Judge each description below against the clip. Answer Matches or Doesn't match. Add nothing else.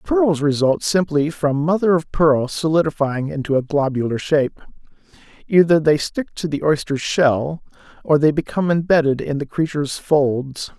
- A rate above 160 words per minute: Doesn't match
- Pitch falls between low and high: Matches